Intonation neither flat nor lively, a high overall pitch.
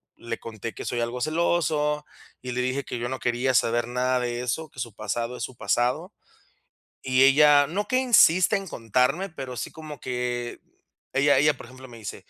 No: average, 3.6 semitones; low, 130 Hz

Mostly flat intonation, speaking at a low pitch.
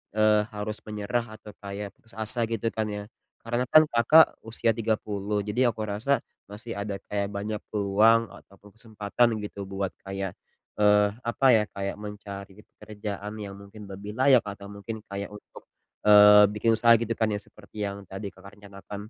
Yes: narrow, 1.8 semitones; low, 105 Hz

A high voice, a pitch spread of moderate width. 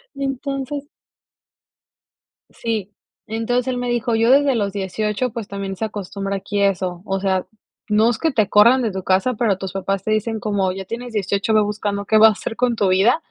Yes: high, 215 Hz; average, 3.4 semitones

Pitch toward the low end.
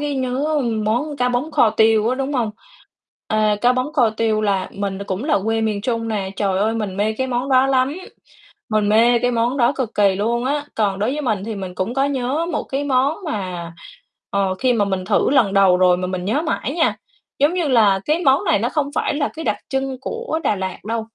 No: high, 235 Hz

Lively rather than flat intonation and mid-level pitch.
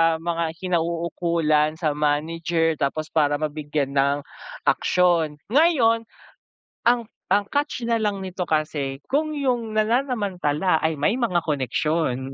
Yes: wide, 6.2 semitones; medium, 165 Hz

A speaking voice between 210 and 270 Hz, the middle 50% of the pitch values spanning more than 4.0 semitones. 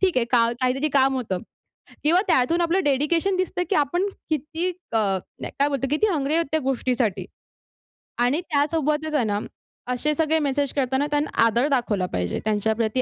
No: very high, 280 Hz; average, 4.5 semitones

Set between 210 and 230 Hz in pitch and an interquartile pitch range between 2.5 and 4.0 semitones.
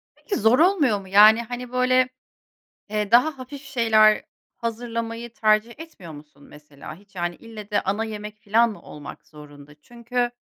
Yes: high, 220 Hz; average, 3.4 semitones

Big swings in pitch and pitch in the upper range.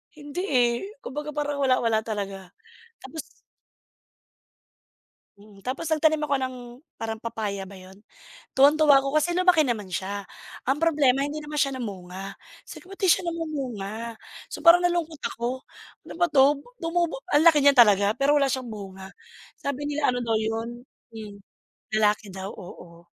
Yes: wide, 6.0 semitones; very high, 260 Hz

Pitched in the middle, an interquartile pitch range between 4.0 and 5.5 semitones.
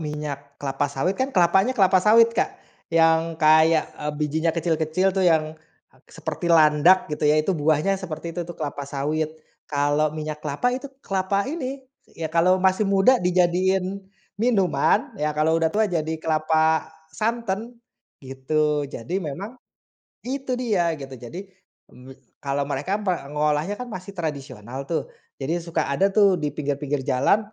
Yes: medium, 165 Hz; average, 4.4 semitones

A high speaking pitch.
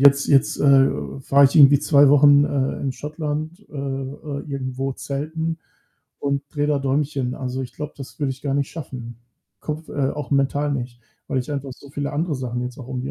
No: medium, 140 Hz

